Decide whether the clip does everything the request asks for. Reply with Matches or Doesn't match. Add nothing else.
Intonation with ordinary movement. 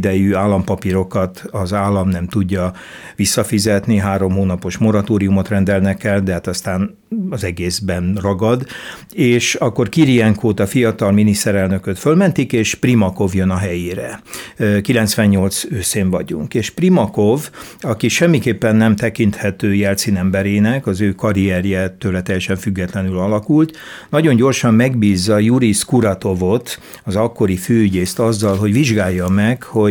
Matches